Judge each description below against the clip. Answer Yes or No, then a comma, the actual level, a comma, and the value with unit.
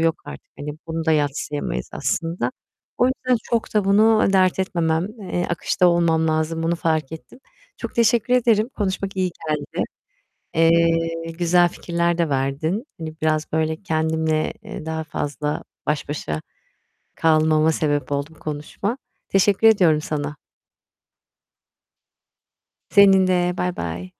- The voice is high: No, medium, 165 Hz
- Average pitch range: Yes, average, 3.2 semitones